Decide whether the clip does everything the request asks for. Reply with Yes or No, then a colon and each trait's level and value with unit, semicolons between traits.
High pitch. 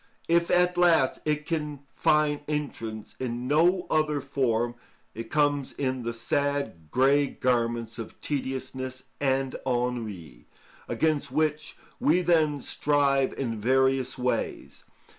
No: low, 135 Hz